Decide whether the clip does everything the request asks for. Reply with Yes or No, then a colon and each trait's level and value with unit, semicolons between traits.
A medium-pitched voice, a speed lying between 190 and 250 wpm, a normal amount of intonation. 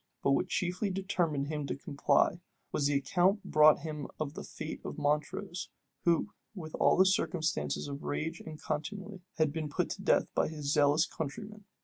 No: medium, 155 Hz; average, 175 wpm; average, 3.9 semitones